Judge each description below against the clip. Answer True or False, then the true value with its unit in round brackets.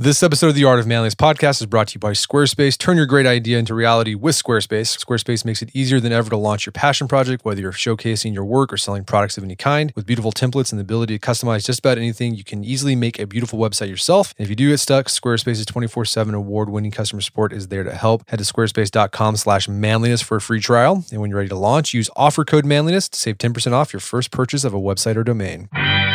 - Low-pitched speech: True (115 Hz)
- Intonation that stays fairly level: False (3.8 semitones)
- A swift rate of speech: True (245 wpm)